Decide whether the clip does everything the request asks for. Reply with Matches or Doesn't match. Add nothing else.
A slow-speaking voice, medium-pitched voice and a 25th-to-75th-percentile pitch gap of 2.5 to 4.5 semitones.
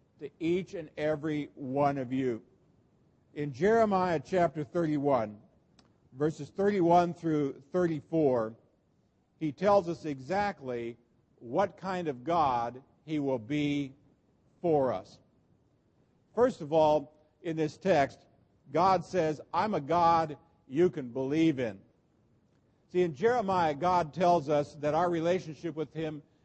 Matches